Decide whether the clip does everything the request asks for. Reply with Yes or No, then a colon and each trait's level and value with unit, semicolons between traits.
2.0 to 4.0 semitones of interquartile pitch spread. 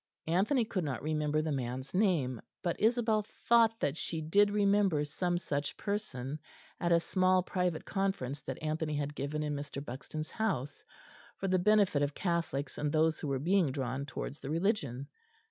No: wide, 5.4 semitones